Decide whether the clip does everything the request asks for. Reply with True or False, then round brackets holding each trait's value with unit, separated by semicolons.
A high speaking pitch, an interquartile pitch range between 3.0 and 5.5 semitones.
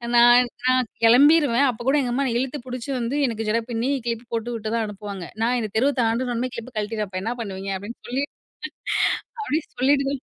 False (240 Hz; 2.6 semitones)